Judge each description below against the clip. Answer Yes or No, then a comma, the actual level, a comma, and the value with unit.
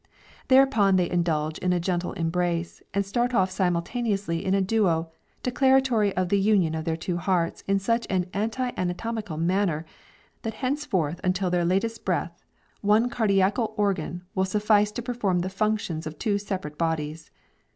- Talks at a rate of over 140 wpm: Yes, average, 160 wpm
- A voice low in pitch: No, high, 190 Hz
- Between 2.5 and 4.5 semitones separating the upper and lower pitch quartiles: Yes, average, 4.0 semitones